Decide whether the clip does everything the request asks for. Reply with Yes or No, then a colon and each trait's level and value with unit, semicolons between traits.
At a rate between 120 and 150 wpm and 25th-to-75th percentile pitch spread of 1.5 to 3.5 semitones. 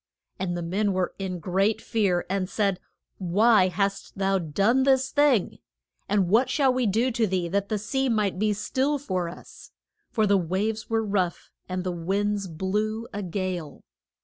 No: average, 175 wpm; average, 3.2 semitones